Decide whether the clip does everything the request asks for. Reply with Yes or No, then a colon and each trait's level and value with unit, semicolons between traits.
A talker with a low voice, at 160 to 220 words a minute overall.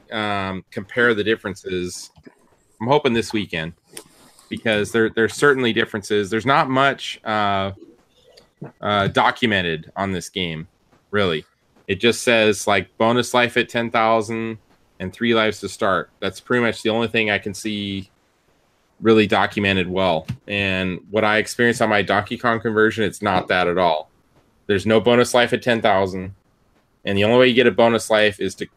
Yes: low, 110 Hz; average, 165 wpm